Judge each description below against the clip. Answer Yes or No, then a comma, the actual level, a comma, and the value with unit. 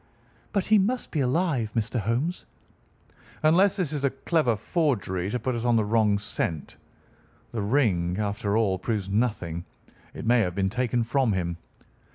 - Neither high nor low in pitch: No, low, 115 Hz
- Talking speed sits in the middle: Yes, average, 165 wpm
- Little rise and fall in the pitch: No, wide, 5.5 semitones